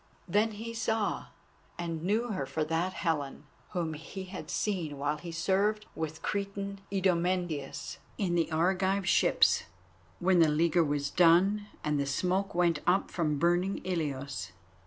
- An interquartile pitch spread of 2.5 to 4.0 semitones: Yes, average, 3.7 semitones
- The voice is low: No, medium, 175 Hz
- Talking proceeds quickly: No, average, 145 wpm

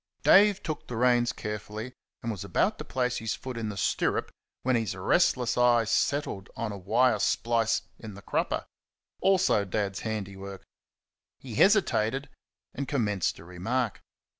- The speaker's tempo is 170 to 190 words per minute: No, average, 150 wpm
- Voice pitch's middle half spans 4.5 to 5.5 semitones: No, average, 3.6 semitones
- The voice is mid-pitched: No, low, 115 Hz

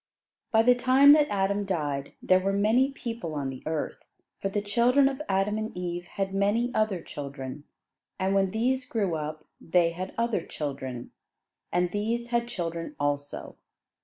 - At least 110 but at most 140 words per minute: No, average, 160 wpm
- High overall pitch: Yes, high, 195 Hz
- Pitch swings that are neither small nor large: No, wide, 6.0 semitones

